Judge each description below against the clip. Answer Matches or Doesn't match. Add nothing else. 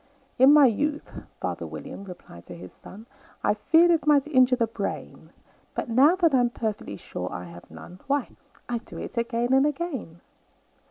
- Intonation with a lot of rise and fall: Matches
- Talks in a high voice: Matches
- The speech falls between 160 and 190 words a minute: Matches